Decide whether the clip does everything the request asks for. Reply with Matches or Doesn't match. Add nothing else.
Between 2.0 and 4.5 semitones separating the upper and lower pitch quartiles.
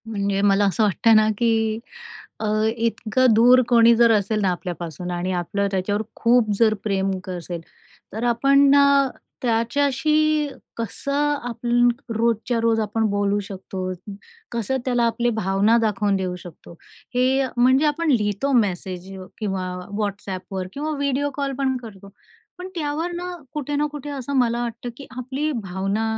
Doesn't match